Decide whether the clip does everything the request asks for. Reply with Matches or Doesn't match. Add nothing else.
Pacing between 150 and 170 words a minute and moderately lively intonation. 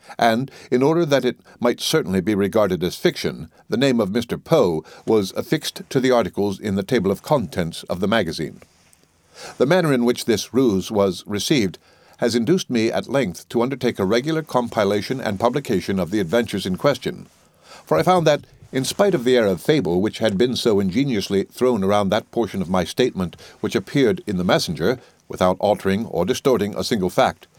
Doesn't match